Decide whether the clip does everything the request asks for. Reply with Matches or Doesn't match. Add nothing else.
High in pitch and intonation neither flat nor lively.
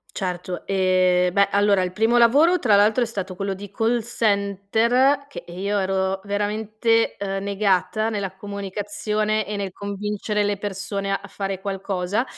Doesn't match